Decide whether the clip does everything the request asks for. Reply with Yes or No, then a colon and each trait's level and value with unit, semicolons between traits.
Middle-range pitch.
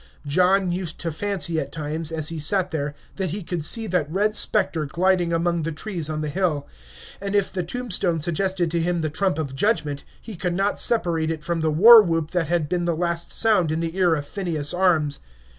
Yes: medium, 170 Hz